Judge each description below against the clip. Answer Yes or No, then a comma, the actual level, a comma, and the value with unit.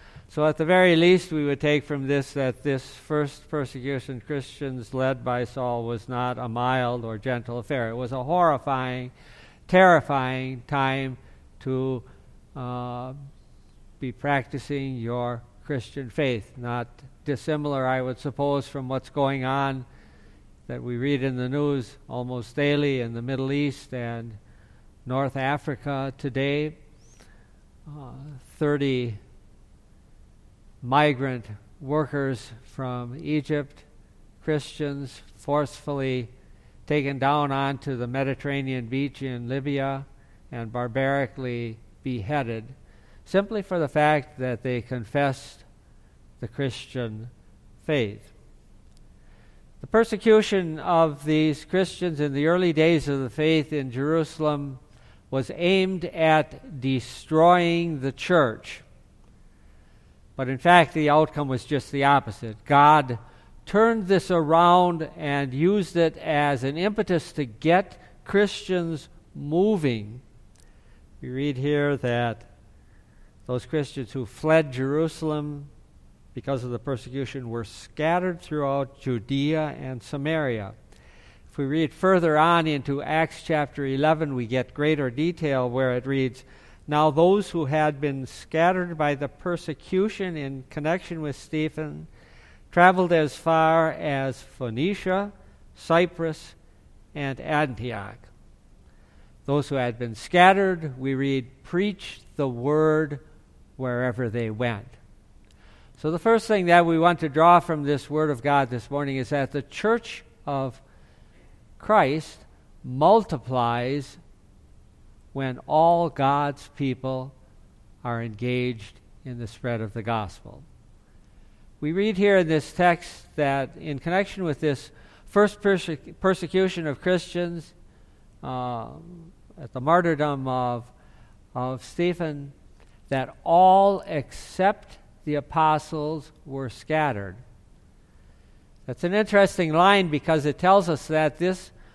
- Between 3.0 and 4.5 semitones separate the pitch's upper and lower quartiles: Yes, average, 4.0 semitones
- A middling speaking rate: No, slow, 120 wpm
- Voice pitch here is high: No, medium, 140 Hz